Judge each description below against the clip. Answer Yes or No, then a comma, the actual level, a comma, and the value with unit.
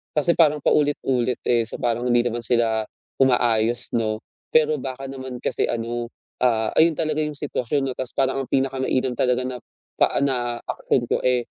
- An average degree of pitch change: No, narrow, 2.3 semitones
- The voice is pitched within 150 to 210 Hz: No, low, 125 Hz